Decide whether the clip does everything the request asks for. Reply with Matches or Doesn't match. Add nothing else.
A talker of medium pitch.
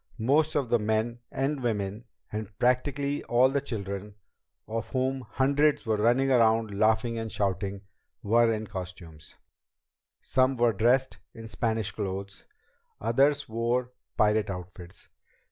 Doesn't match